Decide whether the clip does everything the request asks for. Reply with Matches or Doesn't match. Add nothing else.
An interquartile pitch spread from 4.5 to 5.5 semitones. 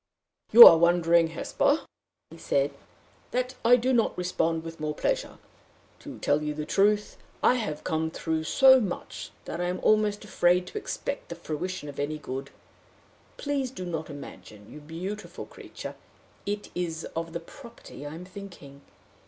Matches